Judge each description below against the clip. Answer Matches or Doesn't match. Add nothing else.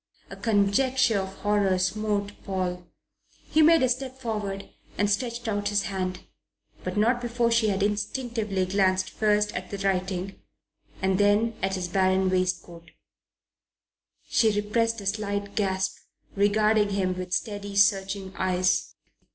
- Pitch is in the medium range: Doesn't match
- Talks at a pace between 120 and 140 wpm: Matches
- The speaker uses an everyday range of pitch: Doesn't match